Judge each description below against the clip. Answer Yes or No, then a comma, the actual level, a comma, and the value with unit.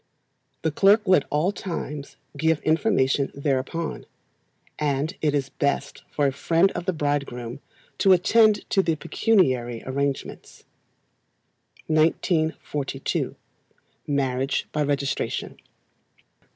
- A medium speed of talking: No, slow, 105 wpm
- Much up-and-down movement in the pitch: No, average, 3.5 semitones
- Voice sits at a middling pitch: Yes, medium, 150 Hz